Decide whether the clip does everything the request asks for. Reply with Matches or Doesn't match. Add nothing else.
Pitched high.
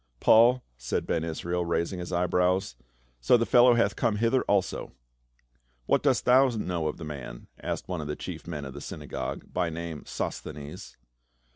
Doesn't match